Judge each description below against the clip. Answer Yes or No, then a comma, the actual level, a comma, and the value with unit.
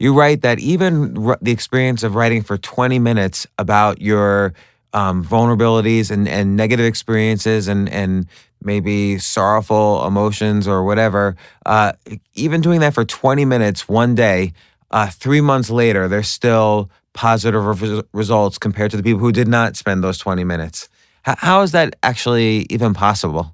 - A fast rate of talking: No, average, 160 wpm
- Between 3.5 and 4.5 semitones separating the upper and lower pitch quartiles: No, average, 2.8 semitones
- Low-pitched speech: Yes, low, 110 Hz